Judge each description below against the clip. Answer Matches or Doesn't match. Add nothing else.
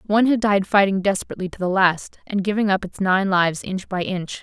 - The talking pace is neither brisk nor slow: Doesn't match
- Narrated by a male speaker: Doesn't match